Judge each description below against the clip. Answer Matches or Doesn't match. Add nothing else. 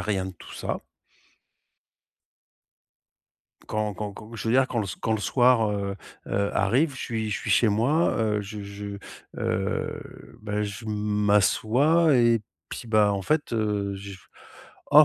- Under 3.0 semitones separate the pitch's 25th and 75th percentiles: Matches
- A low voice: Matches